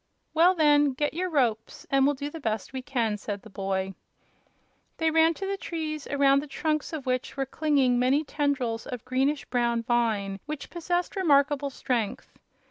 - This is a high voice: Yes, very high, 275 Hz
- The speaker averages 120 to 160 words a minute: No, average, 175 wpm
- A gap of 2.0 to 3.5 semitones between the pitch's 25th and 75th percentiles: No, average, 4.3 semitones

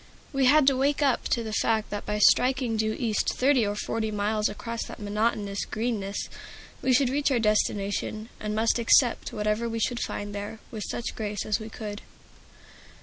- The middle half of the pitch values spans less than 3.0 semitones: Yes, narrow, 2.6 semitones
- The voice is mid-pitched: No, high, 220 Hz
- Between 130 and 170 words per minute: No, average, 185 wpm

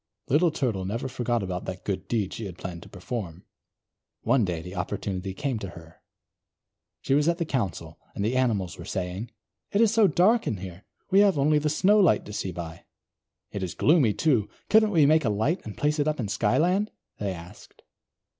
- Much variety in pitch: Yes, wide, 8.5 semitones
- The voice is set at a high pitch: No, low, 115 Hz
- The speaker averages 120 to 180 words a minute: No, average, 195 wpm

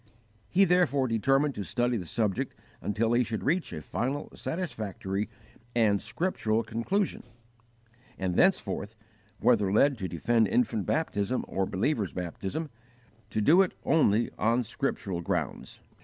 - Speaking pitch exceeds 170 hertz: No, low, 115 Hz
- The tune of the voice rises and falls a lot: Yes, wide, 5.9 semitones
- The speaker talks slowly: Yes, slow, 130 wpm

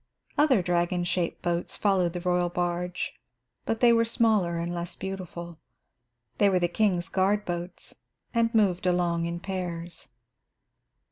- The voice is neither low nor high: Yes, medium, 180 Hz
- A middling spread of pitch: No, narrow, 2.3 semitones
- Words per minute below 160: Yes, average, 140 wpm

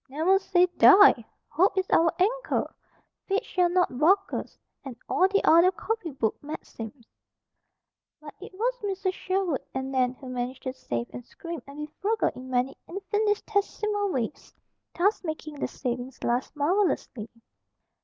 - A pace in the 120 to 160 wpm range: Yes, average, 150 wpm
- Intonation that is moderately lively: No, wide, 7.0 semitones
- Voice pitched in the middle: No, very high, 335 Hz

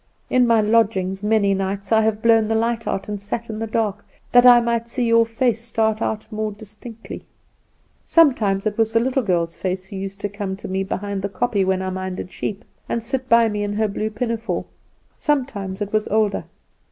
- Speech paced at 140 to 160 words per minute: No, fast, 205 wpm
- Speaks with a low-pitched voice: No, high, 215 Hz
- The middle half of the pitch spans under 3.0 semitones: Yes, narrow, 2.6 semitones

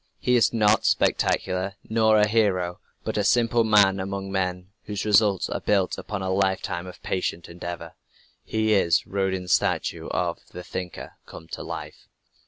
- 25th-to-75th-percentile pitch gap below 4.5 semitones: Yes, narrow, 2.5 semitones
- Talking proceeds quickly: No, average, 160 wpm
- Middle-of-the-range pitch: No, very low, 95 Hz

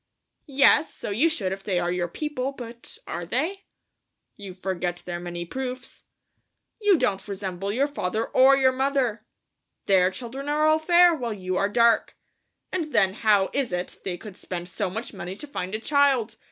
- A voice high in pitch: Yes, high, 225 Hz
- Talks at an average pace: Yes, average, 180 wpm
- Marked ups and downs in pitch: Yes, wide, 6.6 semitones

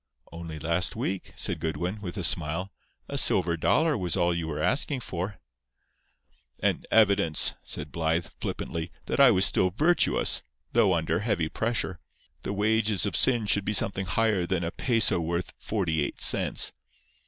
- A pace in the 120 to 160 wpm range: Yes, average, 155 wpm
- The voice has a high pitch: No, very low, 90 Hz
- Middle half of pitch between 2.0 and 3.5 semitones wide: No, average, 4.2 semitones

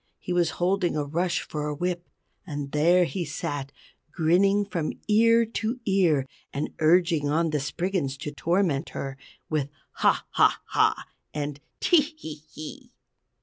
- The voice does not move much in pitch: No, average, 4.5 semitones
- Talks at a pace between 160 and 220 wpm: No, average, 150 wpm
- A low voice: No, medium, 170 Hz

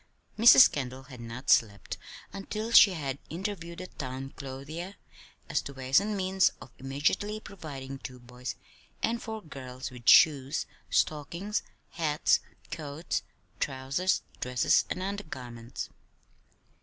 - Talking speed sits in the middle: No, slow, 120 wpm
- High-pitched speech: No, medium, 145 Hz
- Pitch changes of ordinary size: No, wide, 6.3 semitones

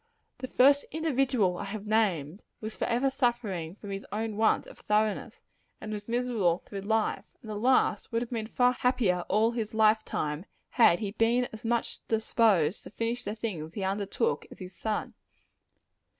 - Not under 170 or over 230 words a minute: Yes, average, 175 wpm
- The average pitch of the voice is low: No, high, 220 Hz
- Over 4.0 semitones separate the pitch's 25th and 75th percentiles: No, average, 3.2 semitones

